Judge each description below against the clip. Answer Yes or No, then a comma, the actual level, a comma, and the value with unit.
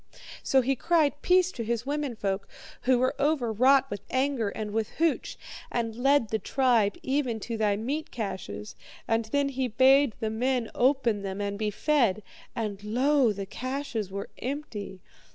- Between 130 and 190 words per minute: Yes, average, 155 wpm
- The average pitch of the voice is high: Yes, high, 240 Hz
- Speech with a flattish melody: No, average, 4.4 semitones